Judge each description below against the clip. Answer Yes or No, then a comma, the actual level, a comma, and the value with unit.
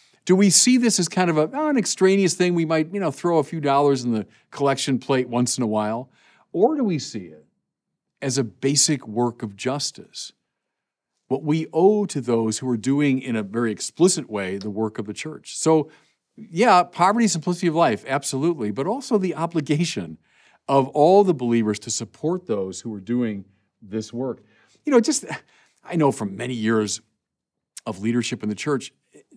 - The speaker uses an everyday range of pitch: No, wide, 7.3 semitones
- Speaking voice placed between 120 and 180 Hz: Yes, low, 135 Hz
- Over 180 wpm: Yes, average, 190 wpm